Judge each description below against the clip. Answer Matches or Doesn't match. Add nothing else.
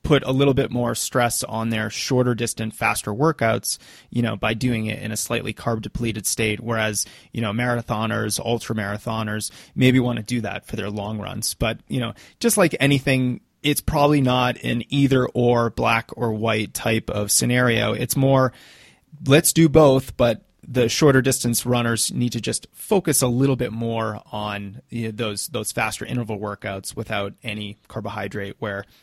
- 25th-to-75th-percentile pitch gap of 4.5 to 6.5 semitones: Doesn't match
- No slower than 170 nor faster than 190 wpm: Matches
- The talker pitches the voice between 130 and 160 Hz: Doesn't match